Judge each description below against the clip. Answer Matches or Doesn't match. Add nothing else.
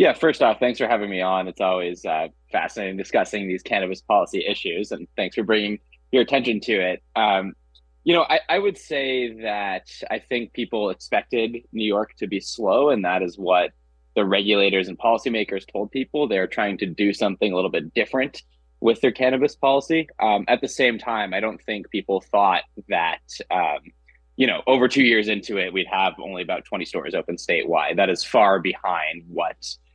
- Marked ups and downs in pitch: Matches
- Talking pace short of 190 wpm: Doesn't match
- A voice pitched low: Matches